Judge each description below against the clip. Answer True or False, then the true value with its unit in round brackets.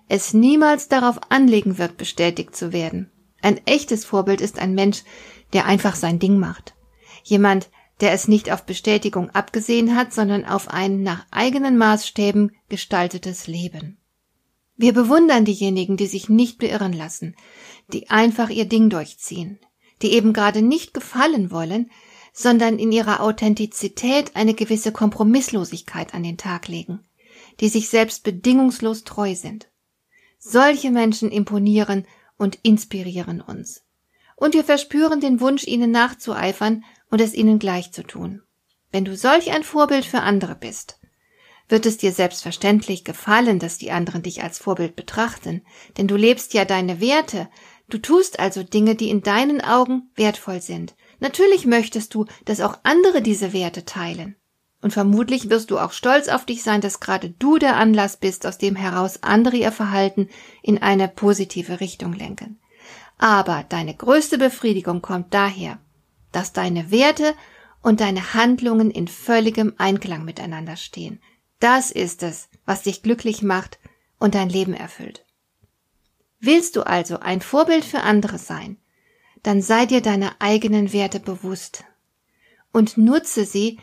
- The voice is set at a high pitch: True (210 Hz)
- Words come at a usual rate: True (150 wpm)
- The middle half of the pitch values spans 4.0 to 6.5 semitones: False (3.5 semitones)